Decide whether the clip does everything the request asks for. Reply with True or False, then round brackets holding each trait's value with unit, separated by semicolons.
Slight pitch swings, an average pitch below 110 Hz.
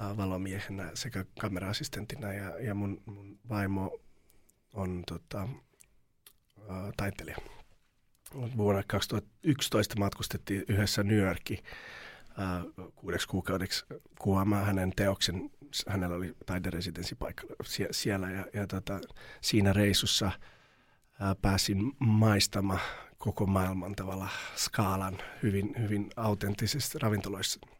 True (1.8 semitones; 100 Hz)